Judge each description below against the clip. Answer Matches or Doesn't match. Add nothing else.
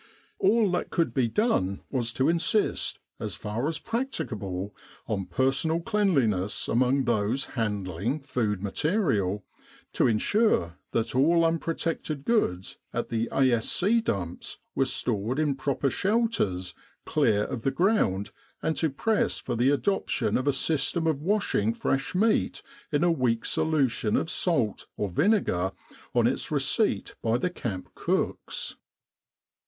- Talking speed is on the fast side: Doesn't match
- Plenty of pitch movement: Matches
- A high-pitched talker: Doesn't match